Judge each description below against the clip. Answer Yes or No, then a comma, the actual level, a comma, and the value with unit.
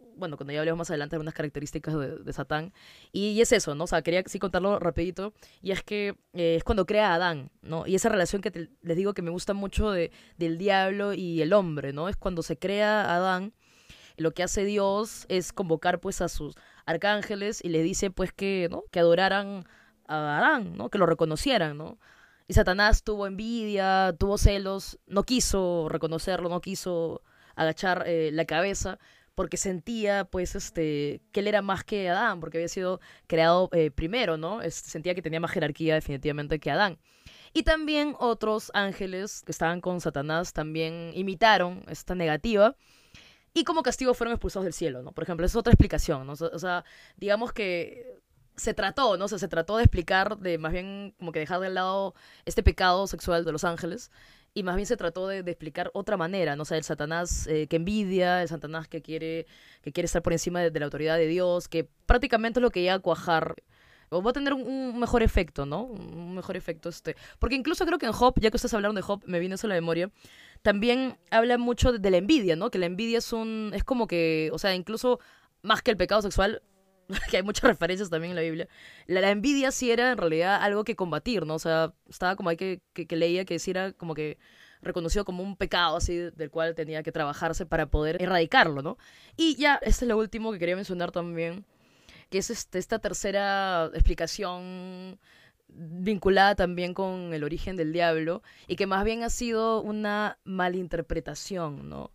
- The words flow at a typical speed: No, fast, 205 wpm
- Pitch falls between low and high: Yes, medium, 180 Hz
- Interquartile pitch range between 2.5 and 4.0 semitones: Yes, average, 3.7 semitones